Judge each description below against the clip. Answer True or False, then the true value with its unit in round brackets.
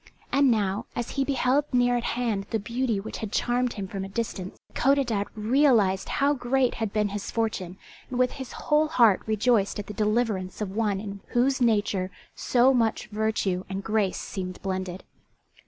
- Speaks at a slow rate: False (175 wpm)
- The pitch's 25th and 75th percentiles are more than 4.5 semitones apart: False (3.9 semitones)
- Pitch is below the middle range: False (220 Hz)